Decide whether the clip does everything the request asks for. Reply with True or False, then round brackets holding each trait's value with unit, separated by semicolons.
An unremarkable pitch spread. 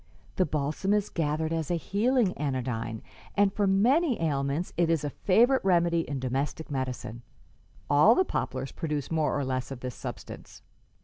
False (5.9 semitones)